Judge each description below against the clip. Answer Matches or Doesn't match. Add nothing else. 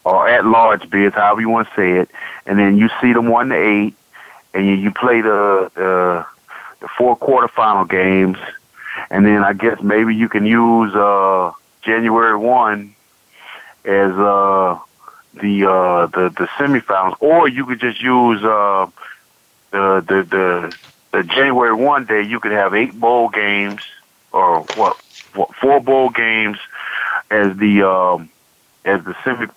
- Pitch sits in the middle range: Doesn't match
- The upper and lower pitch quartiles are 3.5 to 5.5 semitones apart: Doesn't match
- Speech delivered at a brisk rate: Doesn't match